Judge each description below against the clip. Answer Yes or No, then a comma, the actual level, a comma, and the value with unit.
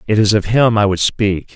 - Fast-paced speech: Yes, fast, 270 wpm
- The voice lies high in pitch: No, low, 105 Hz